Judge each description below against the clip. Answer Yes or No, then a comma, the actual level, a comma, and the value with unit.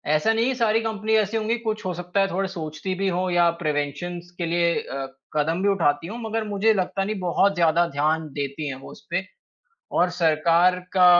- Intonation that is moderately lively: Yes, average, 3.8 semitones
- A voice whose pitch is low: No, medium, 180 Hz